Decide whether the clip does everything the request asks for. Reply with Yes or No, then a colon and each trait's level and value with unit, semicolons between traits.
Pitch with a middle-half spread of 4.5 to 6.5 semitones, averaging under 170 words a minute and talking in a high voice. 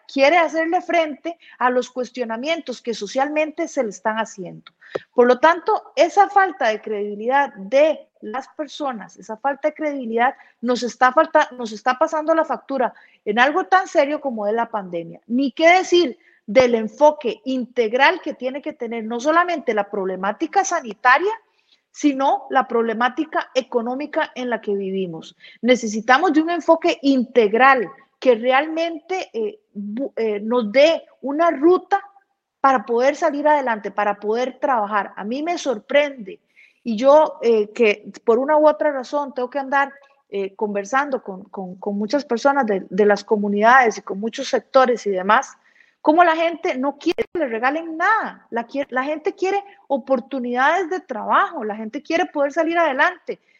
Yes: wide, 5.6 semitones; average, 160 wpm; very high, 270 Hz